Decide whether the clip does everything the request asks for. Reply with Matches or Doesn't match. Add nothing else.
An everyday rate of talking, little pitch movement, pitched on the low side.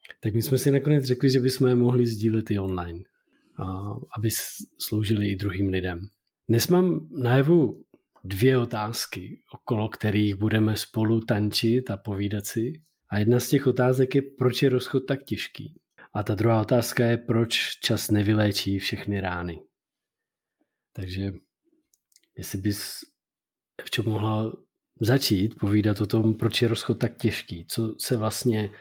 Doesn't match